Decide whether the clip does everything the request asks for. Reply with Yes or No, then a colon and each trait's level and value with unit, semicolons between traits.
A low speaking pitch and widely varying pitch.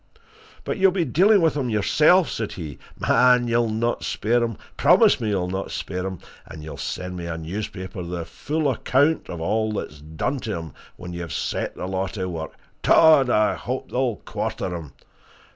Yes: low, 105 Hz; wide, 6.4 semitones